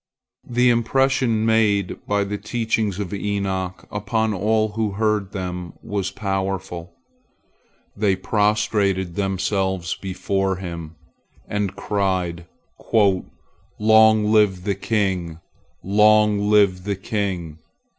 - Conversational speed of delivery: No, slow, 100 wpm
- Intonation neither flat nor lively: No, narrow, 2.1 semitones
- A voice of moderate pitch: No, low, 100 Hz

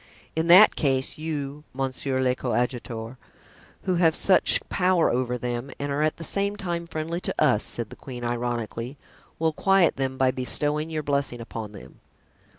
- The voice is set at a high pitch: No, medium, 140 Hz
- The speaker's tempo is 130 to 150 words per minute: No, average, 165 wpm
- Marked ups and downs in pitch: No, average, 4.8 semitones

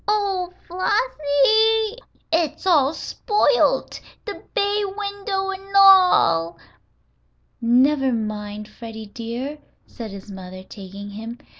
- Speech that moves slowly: Yes, slow, 100 wpm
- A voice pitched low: No, very high, 300 Hz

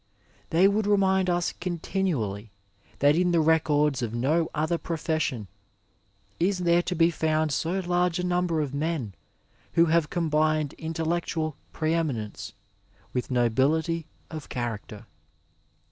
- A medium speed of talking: No, slow, 130 wpm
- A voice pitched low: No, medium, 160 Hz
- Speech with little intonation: No, average, 3.1 semitones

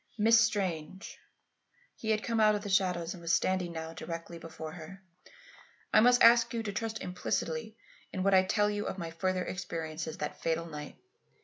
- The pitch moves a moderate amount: Yes, average, 4.3 semitones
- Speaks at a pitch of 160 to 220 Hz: Yes, medium, 185 Hz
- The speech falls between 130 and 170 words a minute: No, average, 185 wpm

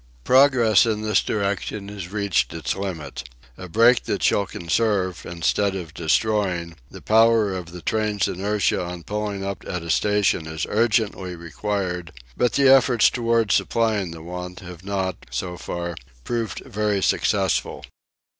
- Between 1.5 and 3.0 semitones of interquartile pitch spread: No, average, 3.5 semitones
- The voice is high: No, low, 100 Hz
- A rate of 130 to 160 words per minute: Yes, average, 145 wpm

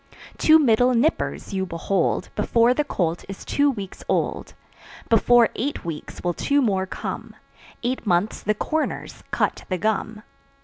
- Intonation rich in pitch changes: No, average, 5.0 semitones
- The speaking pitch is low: No, high, 220 Hz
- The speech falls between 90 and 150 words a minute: Yes, average, 145 wpm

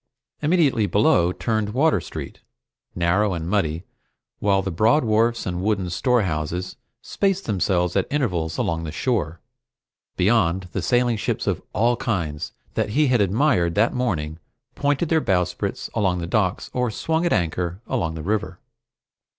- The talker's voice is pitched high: No, low, 100 Hz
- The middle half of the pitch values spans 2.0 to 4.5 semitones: No, wide, 5.6 semitones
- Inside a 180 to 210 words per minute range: No, average, 150 wpm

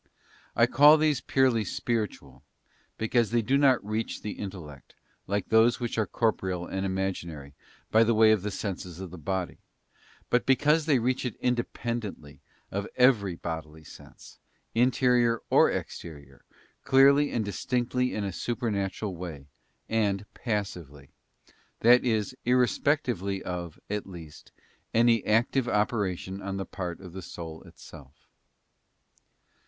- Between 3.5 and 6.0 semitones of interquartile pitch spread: Yes, average, 4.9 semitones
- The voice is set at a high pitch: No, low, 105 Hz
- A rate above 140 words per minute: No, slow, 135 wpm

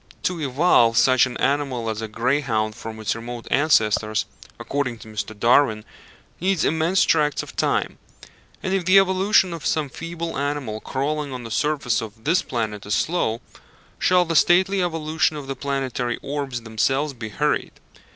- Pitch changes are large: Yes, wide, 5.8 semitones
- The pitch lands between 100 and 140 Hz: Yes, low, 135 Hz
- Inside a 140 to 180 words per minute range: Yes, average, 160 wpm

